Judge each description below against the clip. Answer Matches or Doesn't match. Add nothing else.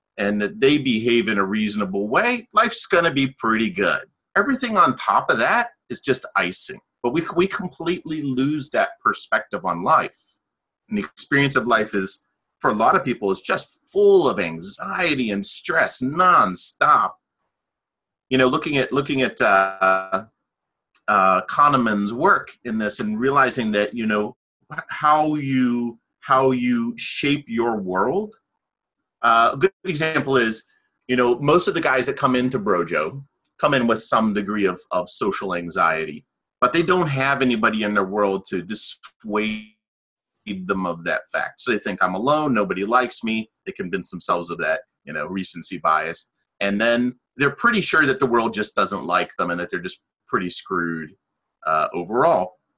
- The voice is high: Doesn't match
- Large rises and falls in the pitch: Matches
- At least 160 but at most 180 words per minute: Matches